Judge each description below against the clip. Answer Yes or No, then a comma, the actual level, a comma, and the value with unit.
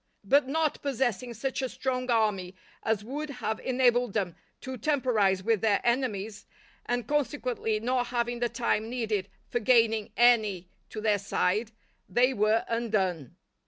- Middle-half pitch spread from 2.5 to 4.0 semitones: Yes, average, 3.1 semitones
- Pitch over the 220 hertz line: Yes, high, 235 Hz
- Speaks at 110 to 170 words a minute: Yes, average, 145 wpm